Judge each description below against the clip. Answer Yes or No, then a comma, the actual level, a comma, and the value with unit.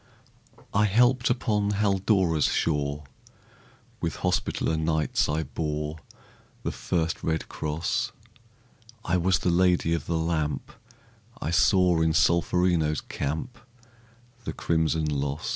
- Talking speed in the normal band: No, slow, 110 wpm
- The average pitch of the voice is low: Yes, very low, 80 Hz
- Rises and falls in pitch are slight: No, average, 3.0 semitones